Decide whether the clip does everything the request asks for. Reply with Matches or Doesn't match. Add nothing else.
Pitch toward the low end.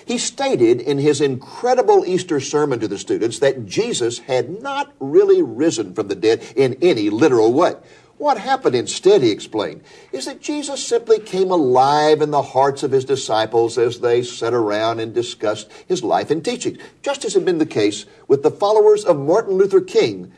Doesn't match